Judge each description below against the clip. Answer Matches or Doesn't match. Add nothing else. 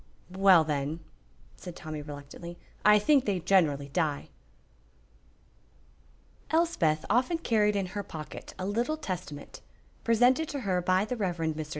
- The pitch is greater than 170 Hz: Matches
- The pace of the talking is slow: Matches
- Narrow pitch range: Doesn't match